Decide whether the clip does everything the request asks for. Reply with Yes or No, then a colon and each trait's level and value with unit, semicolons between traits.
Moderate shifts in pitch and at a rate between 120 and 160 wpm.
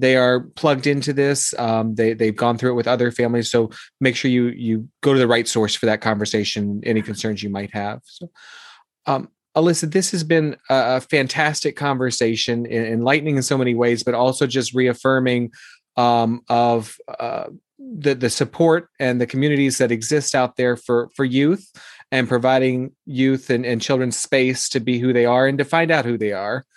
No: average, 3.1 semitones; average, 190 wpm